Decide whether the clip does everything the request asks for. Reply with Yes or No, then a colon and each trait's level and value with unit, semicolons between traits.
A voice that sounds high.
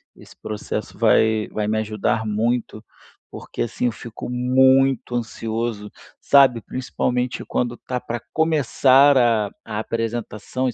No: low, 120 Hz